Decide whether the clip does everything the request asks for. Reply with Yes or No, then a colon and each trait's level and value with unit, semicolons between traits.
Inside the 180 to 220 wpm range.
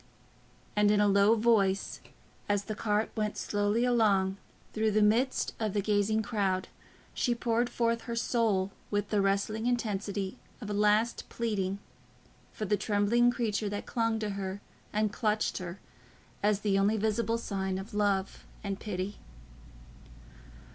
No: average, 150 wpm